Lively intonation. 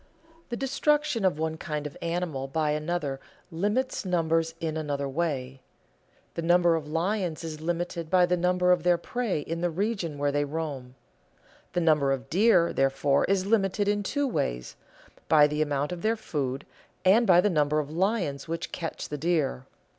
No: average, 3.7 semitones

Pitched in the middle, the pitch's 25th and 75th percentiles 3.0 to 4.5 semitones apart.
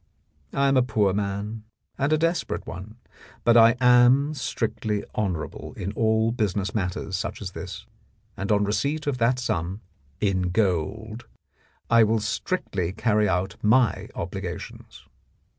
No: low, 110 Hz; average, 3.7 semitones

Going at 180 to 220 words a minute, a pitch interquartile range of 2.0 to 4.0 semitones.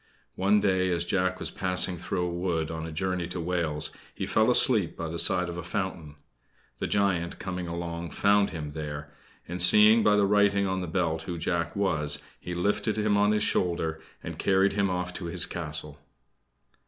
Yes: average, 190 wpm; average, 2.9 semitones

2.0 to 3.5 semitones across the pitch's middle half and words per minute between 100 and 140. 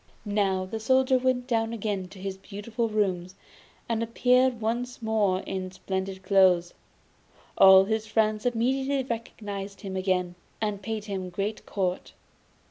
Yes: average, 3.2 semitones; slow, 135 wpm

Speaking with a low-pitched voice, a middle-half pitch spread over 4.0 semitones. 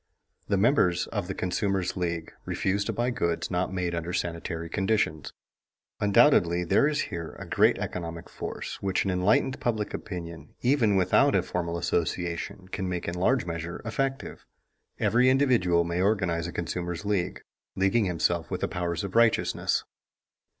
No: very low, 90 Hz; average, 3.6 semitones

